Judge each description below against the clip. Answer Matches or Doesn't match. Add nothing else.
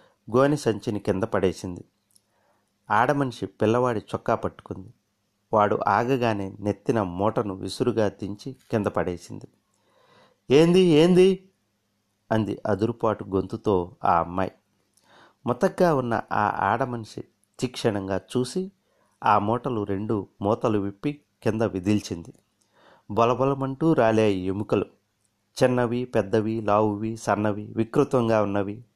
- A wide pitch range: Doesn't match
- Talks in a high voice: Doesn't match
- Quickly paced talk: Doesn't match